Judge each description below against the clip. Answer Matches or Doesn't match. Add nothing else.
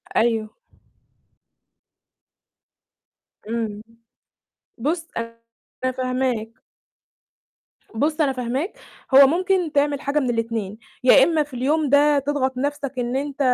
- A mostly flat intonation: Doesn't match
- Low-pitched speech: Doesn't match